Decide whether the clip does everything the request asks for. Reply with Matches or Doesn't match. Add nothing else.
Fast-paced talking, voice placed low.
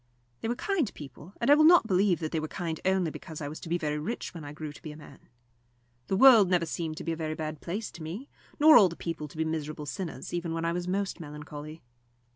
Doesn't match